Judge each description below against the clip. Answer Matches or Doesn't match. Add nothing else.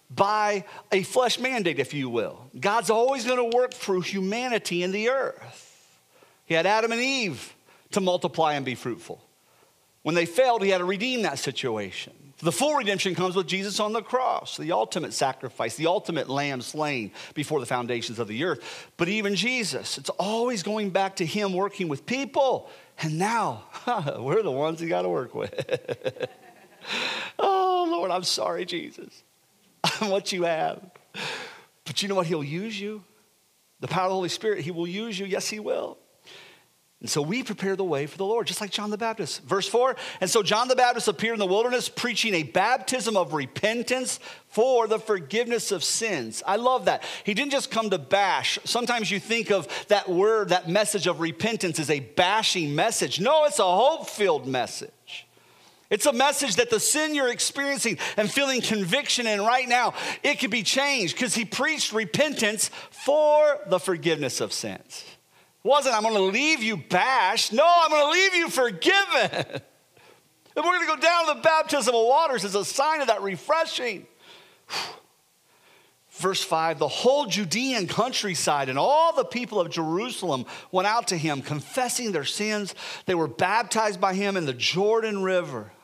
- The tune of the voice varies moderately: Doesn't match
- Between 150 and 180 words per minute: Matches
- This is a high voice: Matches